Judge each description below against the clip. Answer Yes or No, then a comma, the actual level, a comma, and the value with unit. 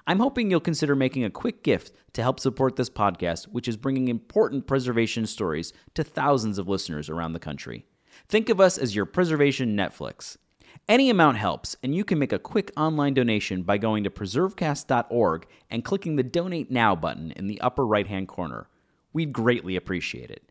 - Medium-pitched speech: No, low, 125 Hz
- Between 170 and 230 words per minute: Yes, average, 185 wpm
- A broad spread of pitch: Yes, wide, 6.6 semitones